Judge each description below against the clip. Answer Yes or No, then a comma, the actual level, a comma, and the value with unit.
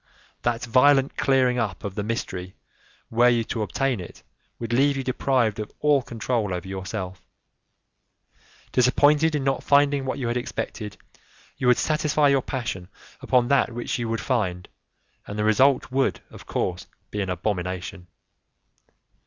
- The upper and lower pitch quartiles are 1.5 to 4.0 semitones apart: No, average, 4.7 semitones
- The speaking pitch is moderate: No, low, 120 Hz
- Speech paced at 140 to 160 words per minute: Yes, average, 155 wpm